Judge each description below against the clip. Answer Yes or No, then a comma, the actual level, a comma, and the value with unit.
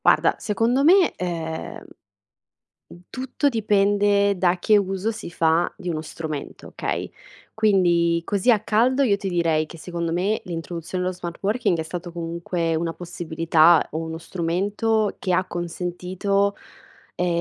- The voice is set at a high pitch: No, medium, 180 Hz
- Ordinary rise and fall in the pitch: Yes, average, 3.4 semitones